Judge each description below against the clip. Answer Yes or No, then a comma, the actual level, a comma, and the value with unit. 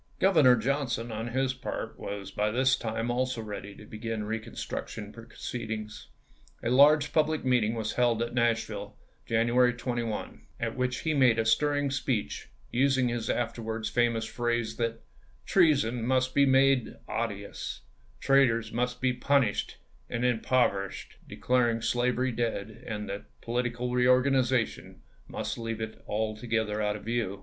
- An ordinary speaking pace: Yes, average, 150 wpm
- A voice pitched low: Yes, low, 120 Hz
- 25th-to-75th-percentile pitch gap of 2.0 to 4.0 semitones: Yes, narrow, 2.4 semitones